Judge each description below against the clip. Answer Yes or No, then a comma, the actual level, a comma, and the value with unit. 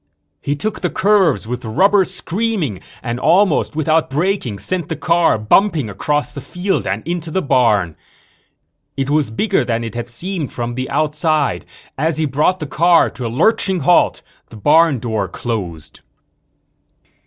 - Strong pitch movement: Yes, wide, 6.9 semitones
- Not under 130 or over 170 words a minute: Yes, average, 155 wpm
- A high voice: No, medium, 150 Hz